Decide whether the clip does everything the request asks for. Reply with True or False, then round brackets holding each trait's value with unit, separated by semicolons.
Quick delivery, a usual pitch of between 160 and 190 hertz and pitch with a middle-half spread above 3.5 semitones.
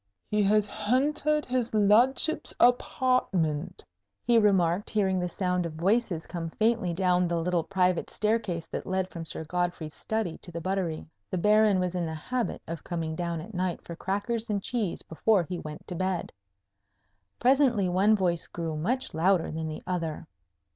False (170 wpm; 185 Hz; 4.3 semitones)